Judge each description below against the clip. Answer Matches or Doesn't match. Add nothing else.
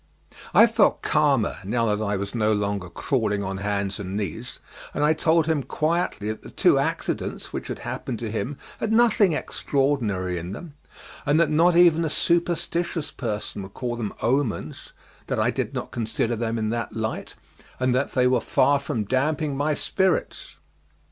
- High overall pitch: Doesn't match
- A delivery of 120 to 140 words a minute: Doesn't match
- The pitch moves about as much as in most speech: Doesn't match